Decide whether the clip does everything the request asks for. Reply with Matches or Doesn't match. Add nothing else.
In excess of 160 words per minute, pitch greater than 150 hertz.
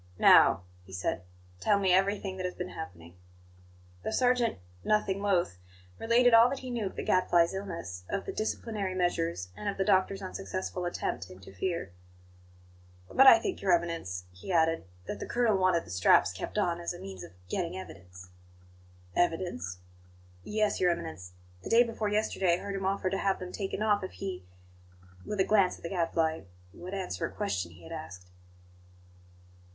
Matches